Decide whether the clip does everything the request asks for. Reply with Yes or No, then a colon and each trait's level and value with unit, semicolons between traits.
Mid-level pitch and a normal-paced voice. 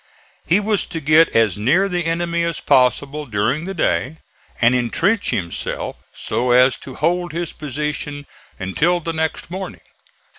Yes: medium, 155 Hz; average, 150 wpm